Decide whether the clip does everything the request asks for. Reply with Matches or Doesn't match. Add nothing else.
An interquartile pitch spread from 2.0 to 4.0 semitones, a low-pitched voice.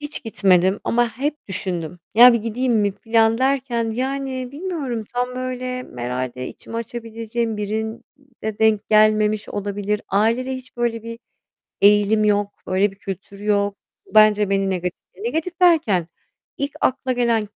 Doesn't match